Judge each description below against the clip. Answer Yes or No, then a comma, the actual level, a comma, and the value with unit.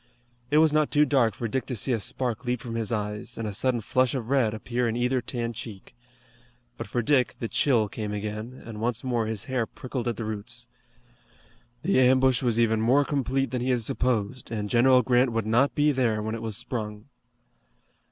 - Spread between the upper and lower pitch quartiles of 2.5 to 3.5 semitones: Yes, average, 2.8 semitones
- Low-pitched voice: Yes, low, 120 Hz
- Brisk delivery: Yes, fast, 210 wpm